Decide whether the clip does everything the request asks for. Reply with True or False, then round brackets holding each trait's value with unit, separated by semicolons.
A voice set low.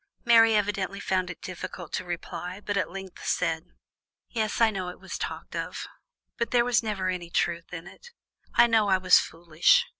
False (190 Hz)